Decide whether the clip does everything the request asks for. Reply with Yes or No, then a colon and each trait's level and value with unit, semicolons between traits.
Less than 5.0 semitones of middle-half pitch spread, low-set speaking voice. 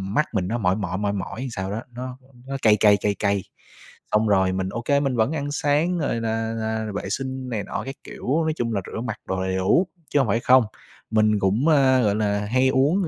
Yes: average, 4.5 semitones; low, 115 Hz